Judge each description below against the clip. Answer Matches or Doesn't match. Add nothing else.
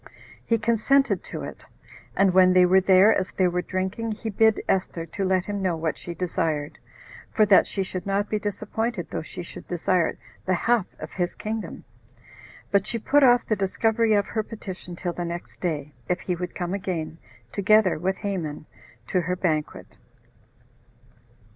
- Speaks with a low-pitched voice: Doesn't match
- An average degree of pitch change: Matches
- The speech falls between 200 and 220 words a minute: Doesn't match